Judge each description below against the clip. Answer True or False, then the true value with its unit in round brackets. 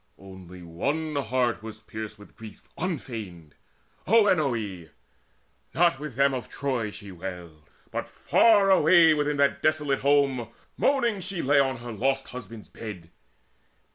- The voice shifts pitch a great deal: True (6.2 semitones)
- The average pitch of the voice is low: True (130 Hz)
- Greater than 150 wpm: False (135 wpm)